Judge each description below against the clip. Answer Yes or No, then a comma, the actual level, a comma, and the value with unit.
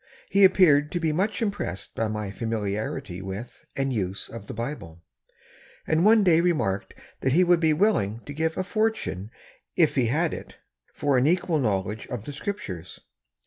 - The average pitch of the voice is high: No, medium, 140 Hz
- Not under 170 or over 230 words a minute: Yes, average, 175 wpm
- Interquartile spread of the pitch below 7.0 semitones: No, wide, 8.8 semitones